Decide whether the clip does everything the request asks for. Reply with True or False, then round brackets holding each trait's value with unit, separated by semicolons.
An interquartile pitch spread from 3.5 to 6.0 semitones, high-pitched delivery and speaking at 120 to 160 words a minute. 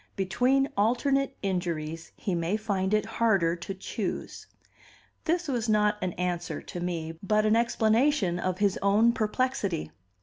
True (4.5 semitones; 205 Hz; 140 wpm)